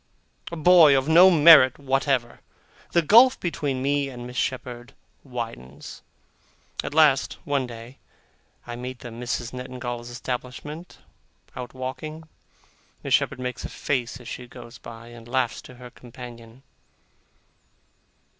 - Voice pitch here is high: No, low, 125 Hz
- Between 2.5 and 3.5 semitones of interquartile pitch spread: Yes, average, 2.9 semitones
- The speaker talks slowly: Yes, slow, 130 wpm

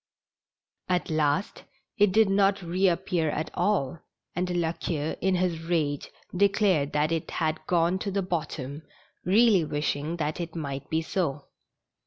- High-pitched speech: No, medium, 170 Hz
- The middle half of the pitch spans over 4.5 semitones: No, average, 3.4 semitones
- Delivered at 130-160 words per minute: Yes, average, 145 wpm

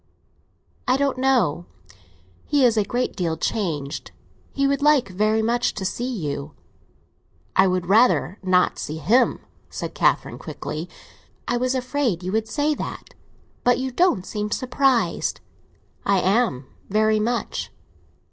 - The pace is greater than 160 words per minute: No, slow, 135 wpm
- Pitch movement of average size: No, wide, 5.7 semitones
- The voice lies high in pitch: Yes, high, 220 Hz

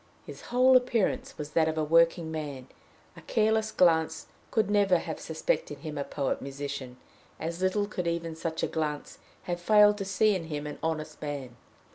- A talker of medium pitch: Yes, medium, 165 Hz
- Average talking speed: Yes, average, 175 wpm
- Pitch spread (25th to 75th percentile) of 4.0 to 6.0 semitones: Yes, average, 5.1 semitones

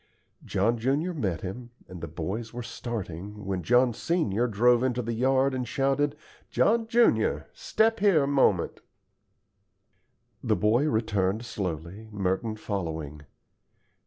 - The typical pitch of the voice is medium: No, low, 115 Hz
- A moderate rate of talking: No, slow, 130 wpm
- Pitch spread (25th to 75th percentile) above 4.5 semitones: Yes, wide, 5.6 semitones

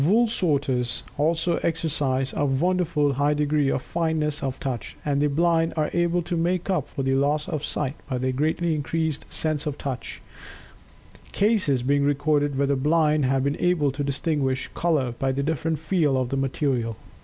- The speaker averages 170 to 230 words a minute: Yes, average, 180 wpm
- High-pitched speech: No, medium, 145 Hz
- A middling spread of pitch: Yes, average, 3.2 semitones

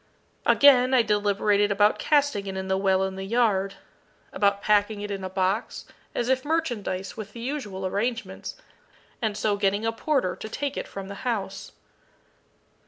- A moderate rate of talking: Yes, average, 170 wpm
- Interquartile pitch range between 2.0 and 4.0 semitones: Yes, average, 3.6 semitones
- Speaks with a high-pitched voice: Yes, high, 205 Hz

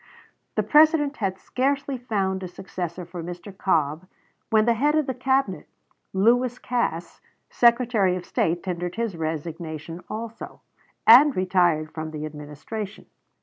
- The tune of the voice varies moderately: No, wide, 6.0 semitones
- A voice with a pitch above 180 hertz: Yes, high, 190 Hz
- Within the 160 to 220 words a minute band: No, slow, 135 wpm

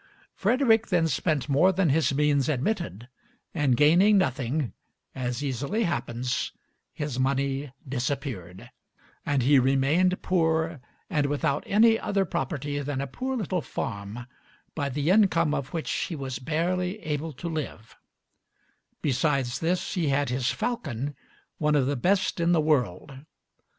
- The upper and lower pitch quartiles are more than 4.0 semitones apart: Yes, average, 4.4 semitones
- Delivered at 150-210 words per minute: No, average, 140 wpm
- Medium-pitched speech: Yes, medium, 145 Hz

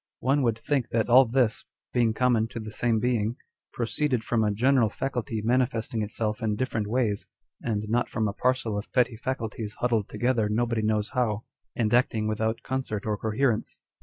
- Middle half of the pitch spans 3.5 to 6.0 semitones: No, narrow, 2.5 semitones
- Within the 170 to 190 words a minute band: Yes, average, 175 wpm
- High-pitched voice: No, low, 115 Hz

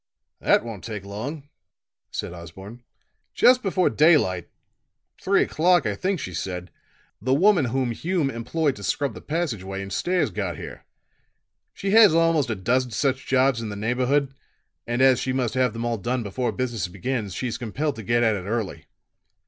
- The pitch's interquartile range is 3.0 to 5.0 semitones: No, wide, 5.6 semitones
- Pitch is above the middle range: No, low, 125 Hz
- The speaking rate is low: No, average, 175 wpm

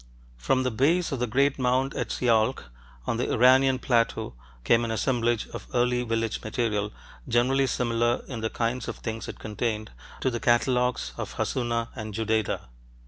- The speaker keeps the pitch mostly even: Yes, narrow, 2.2 semitones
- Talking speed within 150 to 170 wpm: Yes, average, 165 wpm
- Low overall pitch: Yes, low, 120 Hz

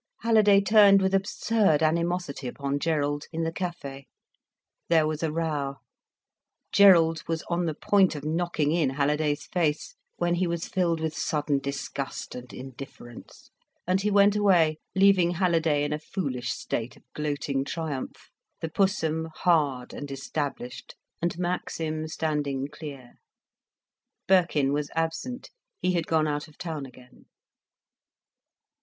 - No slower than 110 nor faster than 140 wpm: Yes, slow, 135 wpm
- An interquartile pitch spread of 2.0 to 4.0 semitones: Yes, average, 3.4 semitones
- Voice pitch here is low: No, medium, 160 Hz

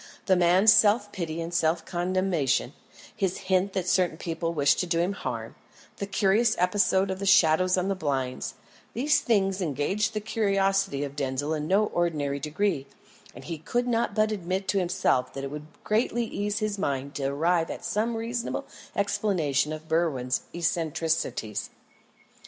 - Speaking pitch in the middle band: Yes, medium, 180 Hz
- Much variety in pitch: No, average, 4.4 semitones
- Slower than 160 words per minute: No, average, 165 wpm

